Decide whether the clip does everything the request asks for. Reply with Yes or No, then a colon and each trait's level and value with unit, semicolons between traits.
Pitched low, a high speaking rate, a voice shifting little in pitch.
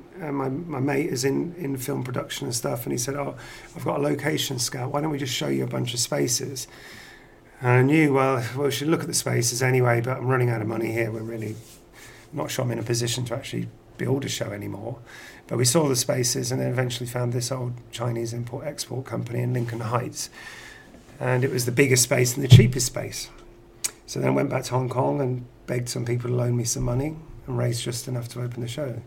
Yes: low, 125 Hz; fast, 240 wpm; narrow, 2.2 semitones